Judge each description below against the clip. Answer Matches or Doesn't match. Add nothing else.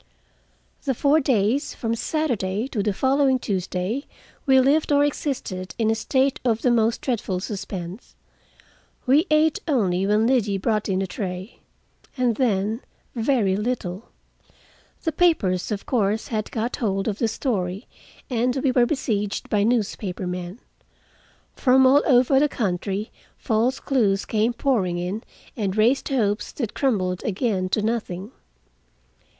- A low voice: Doesn't match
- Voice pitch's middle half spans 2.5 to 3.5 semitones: Doesn't match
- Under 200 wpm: Matches